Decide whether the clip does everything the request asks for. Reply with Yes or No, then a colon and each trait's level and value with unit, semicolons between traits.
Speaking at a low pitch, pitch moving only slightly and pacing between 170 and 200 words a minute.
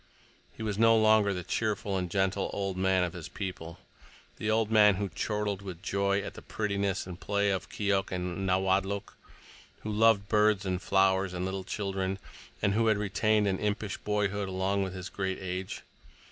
Yes: low, 100 Hz; narrow, 1.7 semitones; average, 180 wpm